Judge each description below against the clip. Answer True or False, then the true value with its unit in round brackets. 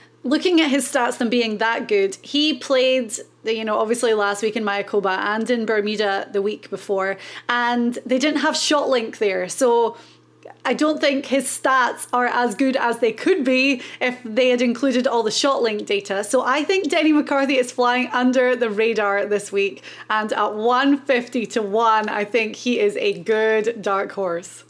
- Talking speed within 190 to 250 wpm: False (180 wpm)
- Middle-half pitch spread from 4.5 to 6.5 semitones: False (3.5 semitones)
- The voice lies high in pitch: True (240 Hz)